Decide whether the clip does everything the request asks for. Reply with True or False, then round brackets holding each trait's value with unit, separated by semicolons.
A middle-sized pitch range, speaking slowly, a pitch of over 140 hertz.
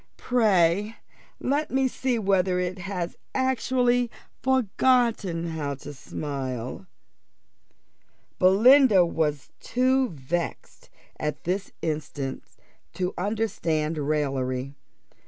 False (8.0 semitones; 90 wpm; 185 Hz)